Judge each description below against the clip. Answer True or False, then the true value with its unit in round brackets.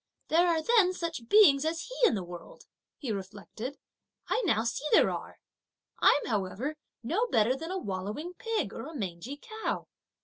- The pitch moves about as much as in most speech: False (8.9 semitones)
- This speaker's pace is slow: False (170 wpm)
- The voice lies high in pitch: True (280 Hz)